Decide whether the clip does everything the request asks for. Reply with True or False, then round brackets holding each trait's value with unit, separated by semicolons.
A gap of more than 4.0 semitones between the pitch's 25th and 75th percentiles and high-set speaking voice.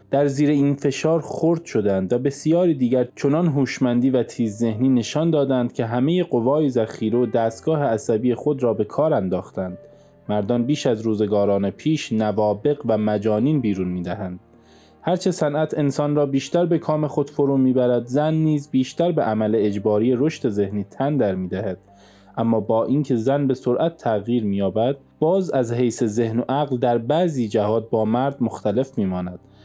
False (5.2 semitones; 125 Hz)